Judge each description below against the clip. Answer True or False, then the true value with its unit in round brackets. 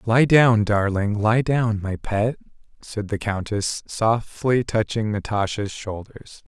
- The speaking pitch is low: True (110 Hz)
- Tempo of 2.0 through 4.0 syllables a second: True (3.6 syllables/s)